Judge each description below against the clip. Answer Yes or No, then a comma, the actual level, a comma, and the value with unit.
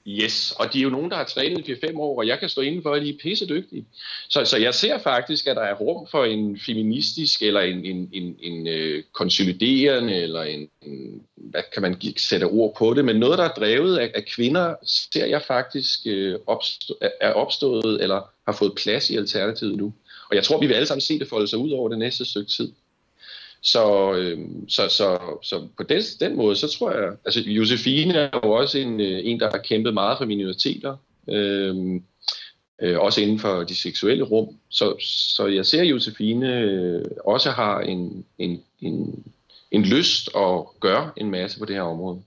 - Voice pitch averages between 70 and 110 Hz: Yes, low, 105 Hz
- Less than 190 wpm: No, average, 200 wpm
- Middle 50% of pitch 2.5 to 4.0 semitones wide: No, average, 5.0 semitones